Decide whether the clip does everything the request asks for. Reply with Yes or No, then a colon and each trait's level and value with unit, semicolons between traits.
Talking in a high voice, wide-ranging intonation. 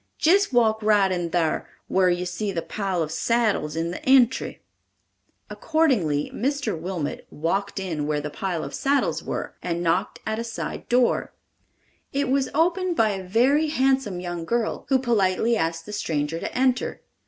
Yes: high, 205 Hz; wide, 6.9 semitones